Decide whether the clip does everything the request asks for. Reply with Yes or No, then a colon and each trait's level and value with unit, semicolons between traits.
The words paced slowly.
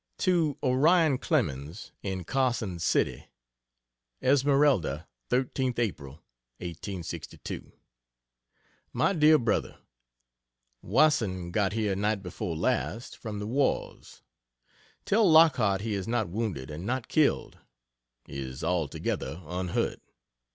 Yes: slow, 100 wpm